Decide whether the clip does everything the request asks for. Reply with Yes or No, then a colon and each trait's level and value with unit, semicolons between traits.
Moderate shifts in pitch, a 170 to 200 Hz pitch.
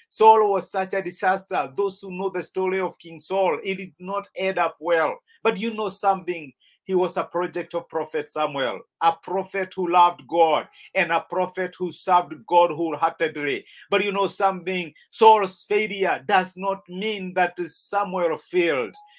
No: narrow, 2.3 semitones; medium, 185 Hz